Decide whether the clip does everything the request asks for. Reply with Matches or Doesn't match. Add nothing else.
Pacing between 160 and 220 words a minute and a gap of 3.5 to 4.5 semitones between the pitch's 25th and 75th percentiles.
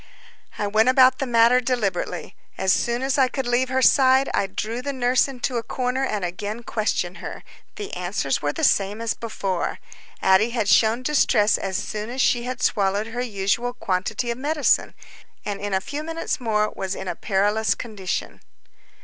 Matches